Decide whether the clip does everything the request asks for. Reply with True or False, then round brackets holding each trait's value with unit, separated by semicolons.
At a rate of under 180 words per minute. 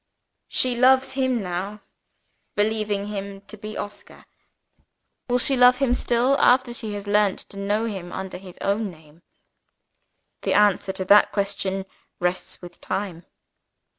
True (140 wpm)